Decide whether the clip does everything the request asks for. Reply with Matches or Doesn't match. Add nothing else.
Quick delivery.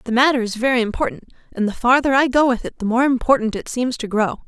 Matches